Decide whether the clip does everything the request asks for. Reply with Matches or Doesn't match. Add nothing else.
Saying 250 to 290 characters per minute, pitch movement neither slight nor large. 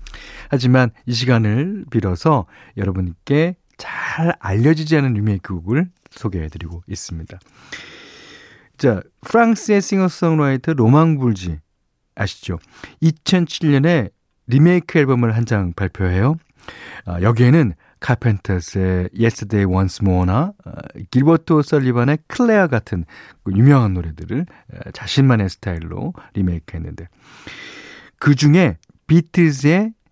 Doesn't match